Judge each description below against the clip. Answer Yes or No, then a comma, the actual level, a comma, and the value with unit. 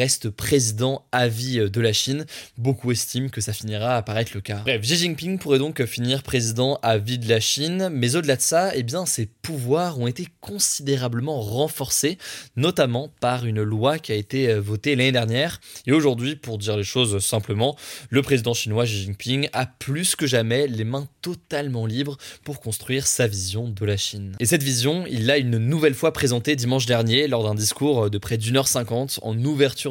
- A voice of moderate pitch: No, low, 125 Hz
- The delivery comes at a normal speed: Yes, average, 195 wpm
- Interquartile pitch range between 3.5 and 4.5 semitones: Yes, average, 3.9 semitones